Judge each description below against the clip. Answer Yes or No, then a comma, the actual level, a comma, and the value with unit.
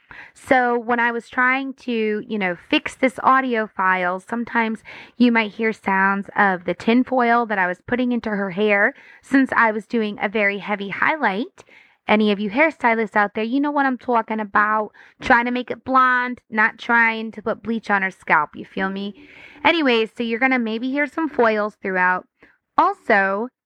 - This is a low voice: No, high, 225 Hz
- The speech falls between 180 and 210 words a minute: Yes, average, 190 wpm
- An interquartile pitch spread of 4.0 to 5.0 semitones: No, average, 3.1 semitones